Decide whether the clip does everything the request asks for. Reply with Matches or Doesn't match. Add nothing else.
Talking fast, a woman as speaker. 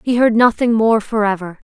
Doesn't match